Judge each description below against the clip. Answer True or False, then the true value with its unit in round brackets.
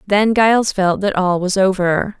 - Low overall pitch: False (195 Hz)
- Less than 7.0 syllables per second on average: True (4.4 syllables/s)